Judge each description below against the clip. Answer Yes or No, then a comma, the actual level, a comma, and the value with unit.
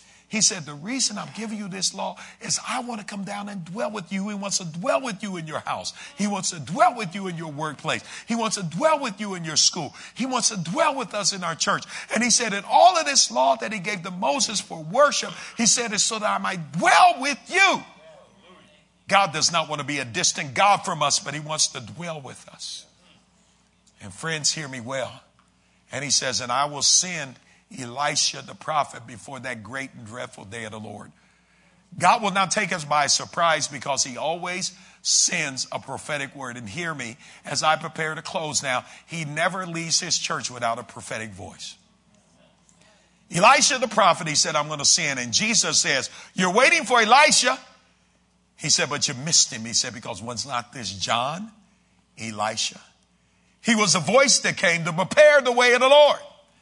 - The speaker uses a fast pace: Yes, fast, 210 wpm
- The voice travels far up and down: Yes, wide, 6.7 semitones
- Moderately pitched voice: Yes, medium, 175 Hz